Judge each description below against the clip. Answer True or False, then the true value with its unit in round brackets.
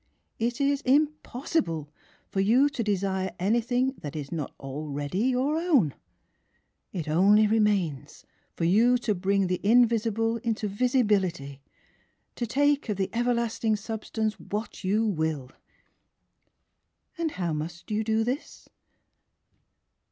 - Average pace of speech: False (125 wpm)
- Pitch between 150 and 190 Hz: False (215 Hz)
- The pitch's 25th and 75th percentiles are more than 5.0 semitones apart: True (5.4 semitones)